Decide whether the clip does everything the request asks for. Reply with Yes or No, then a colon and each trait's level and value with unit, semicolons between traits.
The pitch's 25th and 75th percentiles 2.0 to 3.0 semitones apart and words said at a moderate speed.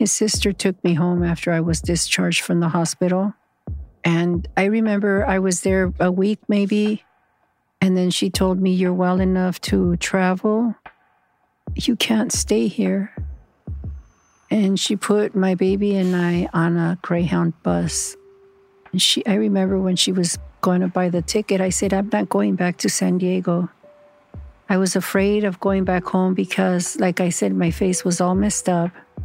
Yes: narrow, 2.5 semitones; average, 170 wpm